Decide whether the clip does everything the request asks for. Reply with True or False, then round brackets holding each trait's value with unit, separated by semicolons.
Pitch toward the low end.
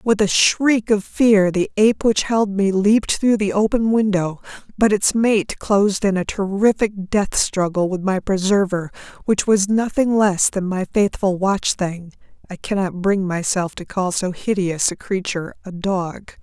False (200 Hz)